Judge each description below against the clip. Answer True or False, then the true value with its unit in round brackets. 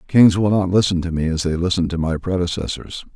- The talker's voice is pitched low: True (90 Hz)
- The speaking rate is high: True (230 wpm)